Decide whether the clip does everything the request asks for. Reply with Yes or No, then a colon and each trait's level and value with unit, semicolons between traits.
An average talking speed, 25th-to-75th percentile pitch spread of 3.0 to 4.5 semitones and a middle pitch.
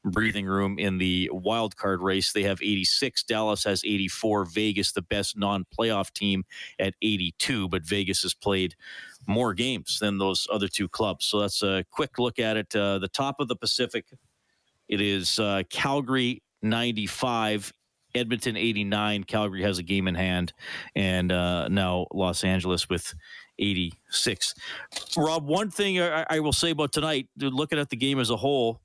No: average, 170 wpm; average, 4.1 semitones; low, 105 Hz